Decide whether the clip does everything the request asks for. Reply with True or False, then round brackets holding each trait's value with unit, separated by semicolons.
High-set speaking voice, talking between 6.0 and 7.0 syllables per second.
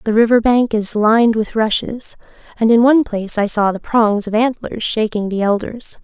False (220 Hz; 5.1 syllables/s)